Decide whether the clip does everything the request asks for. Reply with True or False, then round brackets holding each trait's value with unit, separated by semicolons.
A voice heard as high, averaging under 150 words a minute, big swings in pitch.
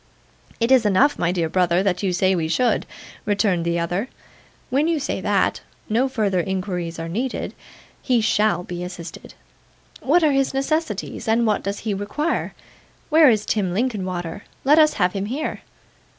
False (205 Hz; 165 wpm; 6.4 semitones)